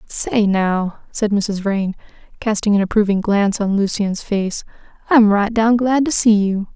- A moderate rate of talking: Yes, average, 170 wpm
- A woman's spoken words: Yes, female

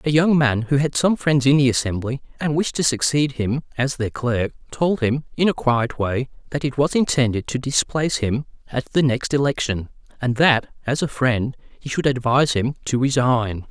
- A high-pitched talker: No, low, 130 Hz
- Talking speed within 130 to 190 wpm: No, average, 200 wpm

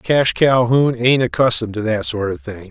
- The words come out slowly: No, average, 200 wpm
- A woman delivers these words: No, male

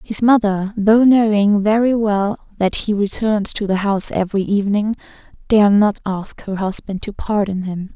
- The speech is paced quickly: No, average, 165 wpm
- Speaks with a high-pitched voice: Yes, high, 205 Hz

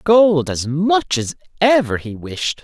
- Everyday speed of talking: Yes, average, 160 wpm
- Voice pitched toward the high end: No, medium, 165 Hz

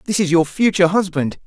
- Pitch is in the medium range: Yes, medium, 180 Hz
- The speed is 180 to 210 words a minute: Yes, fast, 205 wpm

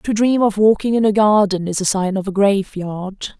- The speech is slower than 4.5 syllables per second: No, 4.8 syllables/s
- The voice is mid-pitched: No, high, 200 Hz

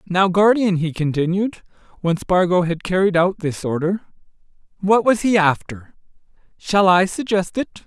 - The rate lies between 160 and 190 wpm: No, average, 145 wpm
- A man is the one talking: Yes, male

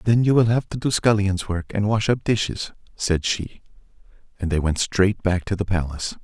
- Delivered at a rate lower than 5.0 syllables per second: No, 5.2 syllables/s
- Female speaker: No, male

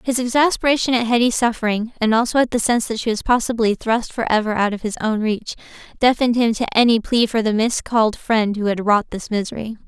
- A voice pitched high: Yes, high, 225 Hz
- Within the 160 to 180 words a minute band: No, fast, 205 wpm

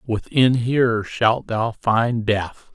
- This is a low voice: Yes, low, 115 Hz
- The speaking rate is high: No, slow, 130 wpm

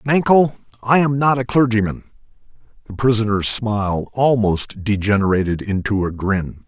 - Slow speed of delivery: Yes, slow, 125 wpm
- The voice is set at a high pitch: No, low, 110 Hz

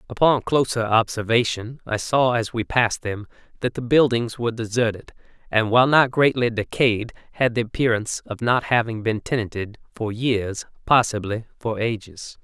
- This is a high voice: No, low, 115 Hz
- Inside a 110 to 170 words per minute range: Yes, average, 155 wpm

